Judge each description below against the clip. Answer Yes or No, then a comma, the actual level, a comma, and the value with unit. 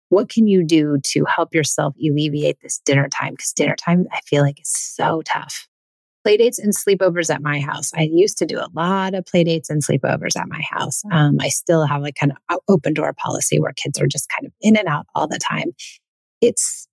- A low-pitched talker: No, medium, 165 Hz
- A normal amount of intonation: Yes, average, 4.5 semitones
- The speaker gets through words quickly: Yes, fast, 220 wpm